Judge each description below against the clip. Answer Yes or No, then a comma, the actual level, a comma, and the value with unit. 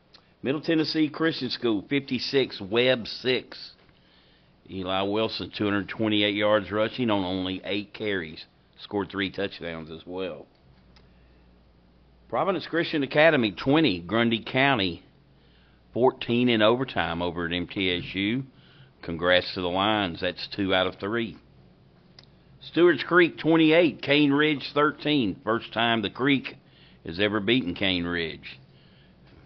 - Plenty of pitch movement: Yes, wide, 6.5 semitones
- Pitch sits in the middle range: No, low, 105 Hz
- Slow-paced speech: Yes, slow, 115 wpm